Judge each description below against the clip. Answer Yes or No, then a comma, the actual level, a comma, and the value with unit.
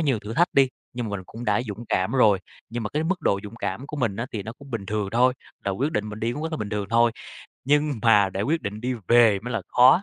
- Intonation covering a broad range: No, average, 4.4 semitones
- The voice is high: No, low, 115 Hz